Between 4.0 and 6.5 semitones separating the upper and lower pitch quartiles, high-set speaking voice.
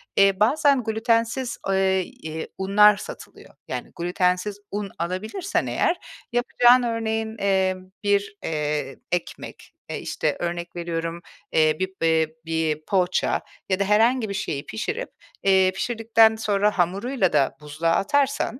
Yes: average, 4.4 semitones; high, 195 Hz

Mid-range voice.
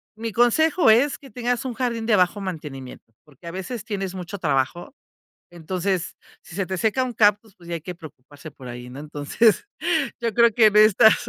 No: high, 195 Hz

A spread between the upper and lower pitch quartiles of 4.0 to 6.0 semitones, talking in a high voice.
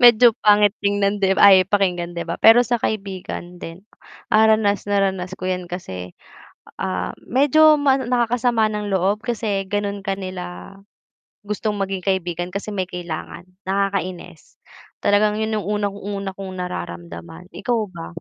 No: average, 2.9 semitones; high, 195 Hz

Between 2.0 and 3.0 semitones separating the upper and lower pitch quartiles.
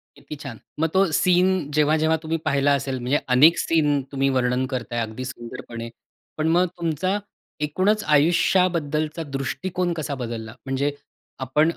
No: average, 4.1 semitones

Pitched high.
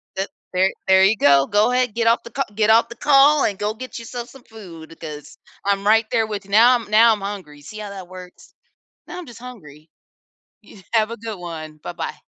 Yes: high, 210 Hz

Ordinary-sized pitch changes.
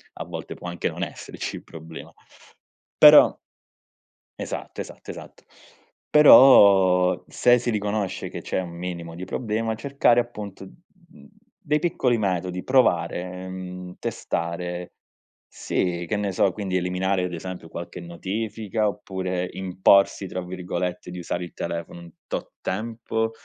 Yes: average, 3.4 semitones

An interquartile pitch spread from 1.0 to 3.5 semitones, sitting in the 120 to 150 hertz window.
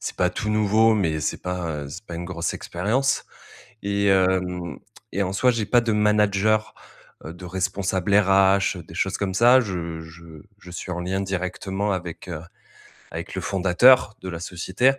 No: average, 2.9 semitones; very low, 95 Hz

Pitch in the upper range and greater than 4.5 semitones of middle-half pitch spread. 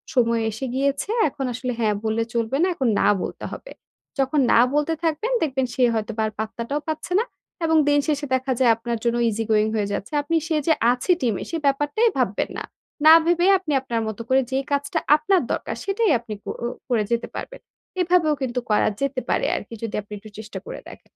Yes: very high, 265 Hz; average, 5.1 semitones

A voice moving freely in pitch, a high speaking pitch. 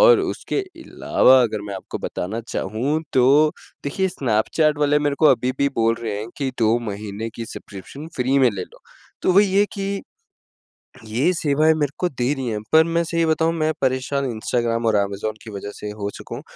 No: wide, 6.1 semitones; low, 130 Hz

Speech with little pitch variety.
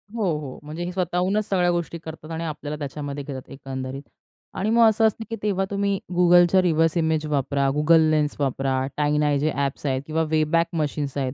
No: average, 3.6 semitones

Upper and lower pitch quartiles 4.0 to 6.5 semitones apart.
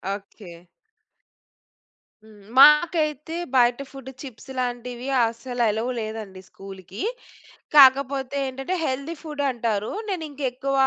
Yes: average, 4.3 semitones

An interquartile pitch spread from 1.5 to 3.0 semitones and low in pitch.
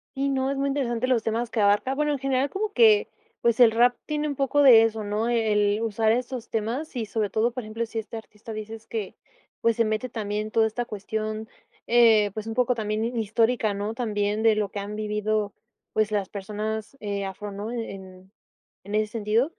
No: narrow, 2.4 semitones; high, 220 Hz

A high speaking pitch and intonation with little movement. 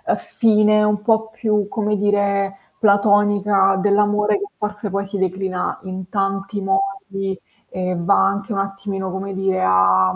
Yes: high, 200 Hz; narrow, 1.4 semitones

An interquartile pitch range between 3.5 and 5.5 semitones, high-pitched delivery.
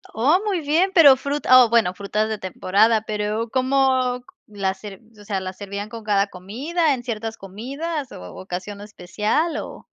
Yes: average, 5.0 semitones; high, 220 Hz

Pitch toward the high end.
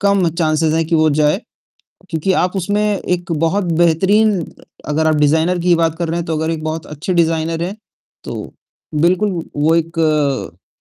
No: medium, 165 Hz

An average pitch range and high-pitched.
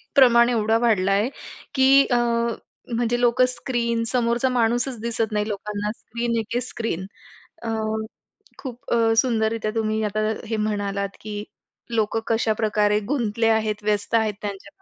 No: narrow, 2.1 semitones; high, 225 Hz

